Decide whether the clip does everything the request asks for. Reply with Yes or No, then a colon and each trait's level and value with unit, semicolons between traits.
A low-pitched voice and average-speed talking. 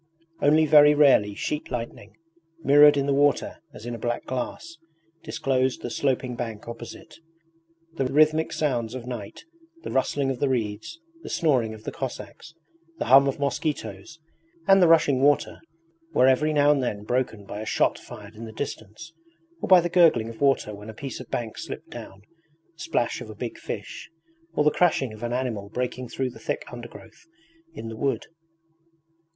Yes: low, 130 Hz; average, 180 wpm